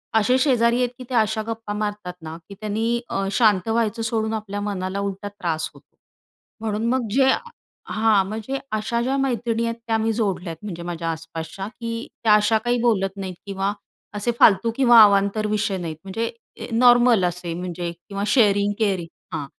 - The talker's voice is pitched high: Yes, high, 210 Hz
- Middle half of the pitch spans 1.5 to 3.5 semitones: Yes, average, 3.0 semitones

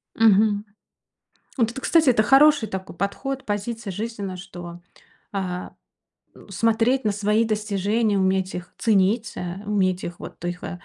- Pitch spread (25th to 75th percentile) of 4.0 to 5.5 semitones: No, average, 3.2 semitones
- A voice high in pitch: Yes, high, 205 Hz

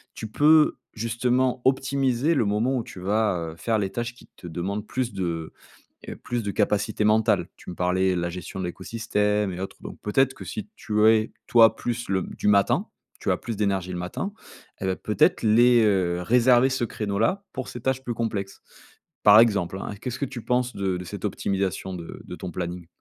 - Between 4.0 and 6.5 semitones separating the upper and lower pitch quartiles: Yes, average, 4.3 semitones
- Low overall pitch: Yes, low, 105 Hz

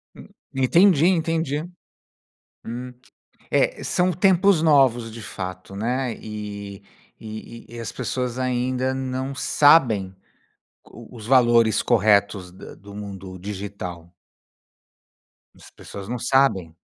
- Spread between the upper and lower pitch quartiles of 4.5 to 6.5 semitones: Yes, average, 4.8 semitones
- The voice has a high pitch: No, low, 120 Hz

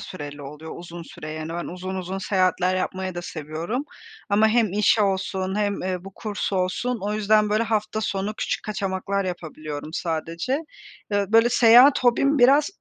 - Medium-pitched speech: No, high, 195 Hz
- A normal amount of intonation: Yes, average, 3.7 semitones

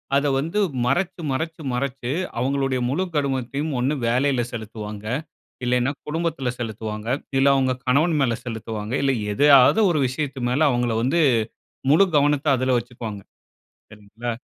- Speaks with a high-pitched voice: No, low, 130 Hz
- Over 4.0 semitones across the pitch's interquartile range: No, average, 3.4 semitones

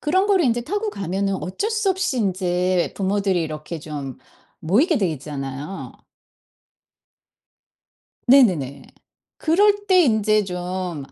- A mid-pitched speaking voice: No, high, 195 Hz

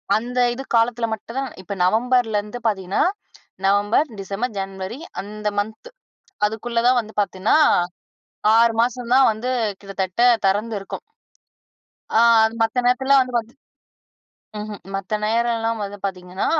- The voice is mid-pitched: No, high, 220 Hz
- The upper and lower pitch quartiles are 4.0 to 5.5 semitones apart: No, average, 3.3 semitones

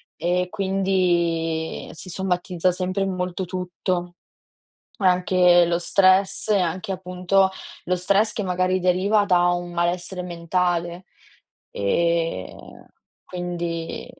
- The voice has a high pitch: No, medium, 180 Hz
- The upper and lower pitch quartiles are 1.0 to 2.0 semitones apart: Yes, narrow, 1.4 semitones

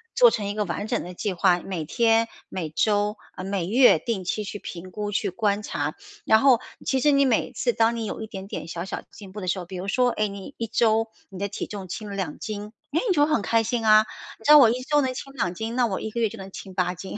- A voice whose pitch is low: No, high, 210 Hz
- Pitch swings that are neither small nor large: Yes, average, 3.5 semitones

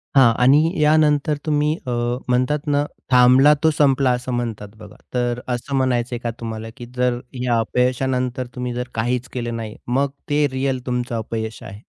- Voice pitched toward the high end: No, low, 125 Hz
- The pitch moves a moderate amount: No, narrow, 2.2 semitones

